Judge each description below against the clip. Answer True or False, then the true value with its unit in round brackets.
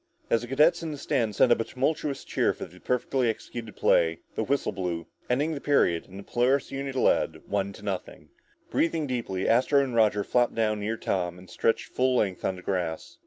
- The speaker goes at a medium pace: False (210 wpm)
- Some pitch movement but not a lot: False (5.7 semitones)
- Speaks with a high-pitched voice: False (115 Hz)